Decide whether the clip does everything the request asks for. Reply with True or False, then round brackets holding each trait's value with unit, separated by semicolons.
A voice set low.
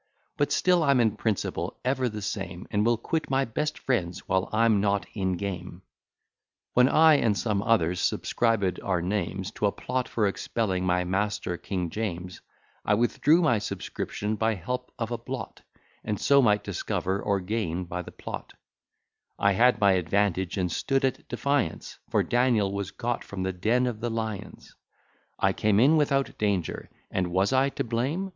True (105 Hz)